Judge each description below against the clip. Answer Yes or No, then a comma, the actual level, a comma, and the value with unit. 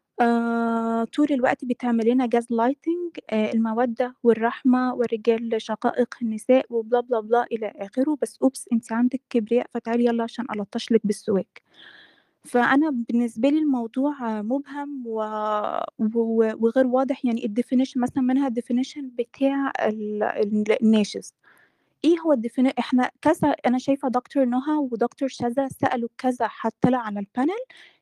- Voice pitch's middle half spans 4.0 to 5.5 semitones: No, narrow, 2.5 semitones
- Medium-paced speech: Yes, average, 125 wpm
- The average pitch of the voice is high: Yes, high, 245 Hz